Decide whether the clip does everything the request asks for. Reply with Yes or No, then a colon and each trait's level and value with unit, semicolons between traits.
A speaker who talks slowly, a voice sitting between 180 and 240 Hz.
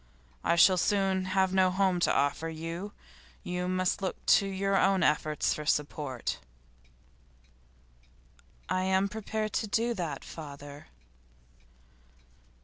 Yes: slow, 120 wpm; medium, 185 Hz